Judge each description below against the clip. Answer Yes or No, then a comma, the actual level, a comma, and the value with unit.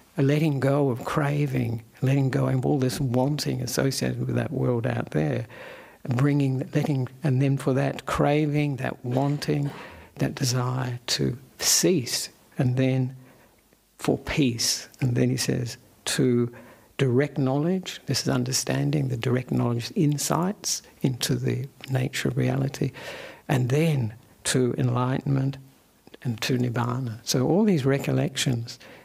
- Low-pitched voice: Yes, low, 130 Hz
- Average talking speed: No, slow, 130 wpm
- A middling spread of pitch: No, narrow, 2.2 semitones